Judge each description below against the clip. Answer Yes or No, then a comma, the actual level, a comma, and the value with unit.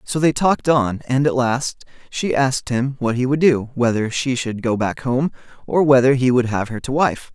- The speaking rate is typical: No, fast, 230 wpm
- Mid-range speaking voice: No, low, 130 Hz